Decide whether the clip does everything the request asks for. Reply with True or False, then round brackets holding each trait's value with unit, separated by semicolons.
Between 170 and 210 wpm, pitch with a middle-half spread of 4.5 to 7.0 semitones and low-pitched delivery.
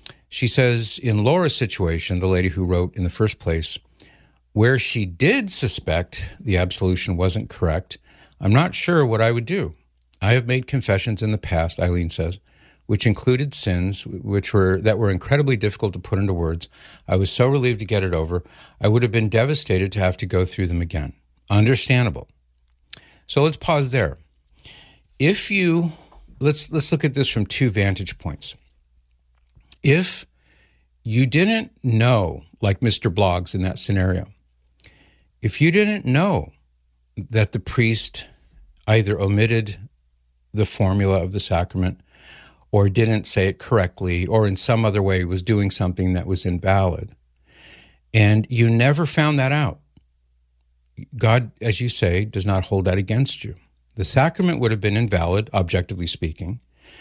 False (160 wpm; 5.1 semitones; 100 Hz)